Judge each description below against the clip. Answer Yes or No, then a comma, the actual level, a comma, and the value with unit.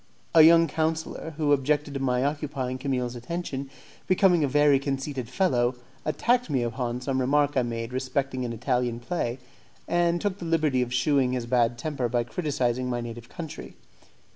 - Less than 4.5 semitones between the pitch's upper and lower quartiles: Yes, average, 3.6 semitones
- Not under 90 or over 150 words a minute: No, average, 165 wpm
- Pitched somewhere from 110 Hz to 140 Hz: Yes, low, 135 Hz